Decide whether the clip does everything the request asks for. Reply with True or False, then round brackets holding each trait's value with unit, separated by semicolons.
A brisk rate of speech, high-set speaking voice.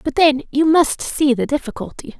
False (190 wpm; 285 Hz)